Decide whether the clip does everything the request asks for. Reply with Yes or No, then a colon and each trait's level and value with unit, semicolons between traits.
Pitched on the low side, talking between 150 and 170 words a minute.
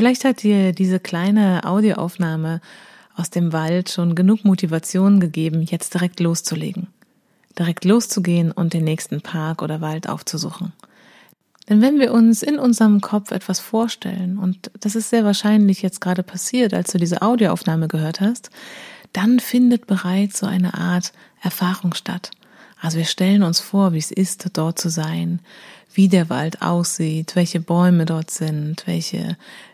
No: medium, 185 Hz; average, 155 wpm